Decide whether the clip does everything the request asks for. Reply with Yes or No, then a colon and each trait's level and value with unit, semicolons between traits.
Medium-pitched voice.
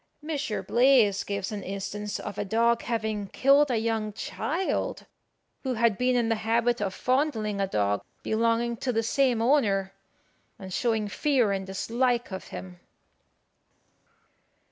No: high, 225 Hz